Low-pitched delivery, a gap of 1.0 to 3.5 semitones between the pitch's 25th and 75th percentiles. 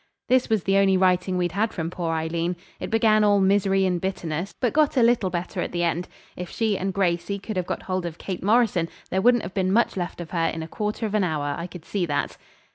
No: medium, 185 Hz; average, 3.1 semitones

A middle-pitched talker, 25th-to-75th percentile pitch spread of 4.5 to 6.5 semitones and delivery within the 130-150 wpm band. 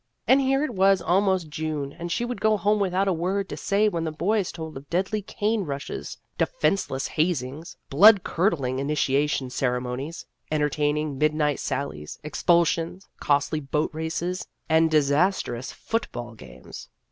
Yes: medium, 160 Hz; average, 5.3 semitones; average, 145 wpm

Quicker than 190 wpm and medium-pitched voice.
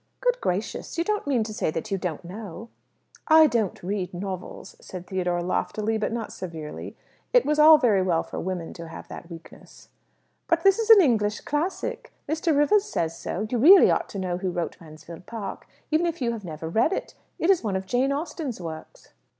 No: average, 200 wpm; high, 215 Hz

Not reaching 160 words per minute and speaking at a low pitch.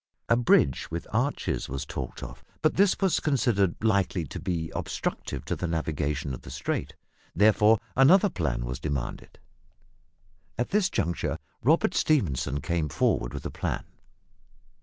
Yes: average, 145 wpm; very low, 90 Hz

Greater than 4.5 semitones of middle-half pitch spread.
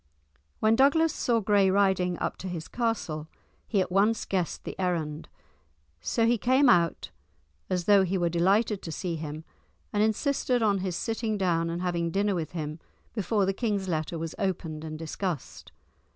No: average, 4.1 semitones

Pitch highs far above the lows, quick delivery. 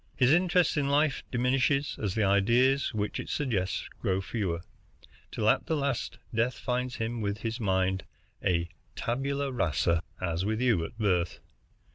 No: wide, 5.7 semitones; average, 155 wpm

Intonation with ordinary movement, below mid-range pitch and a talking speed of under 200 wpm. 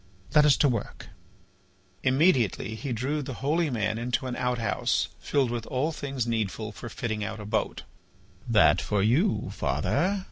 Yes: average, 4.4 semitones; low, 125 Hz; average, 155 wpm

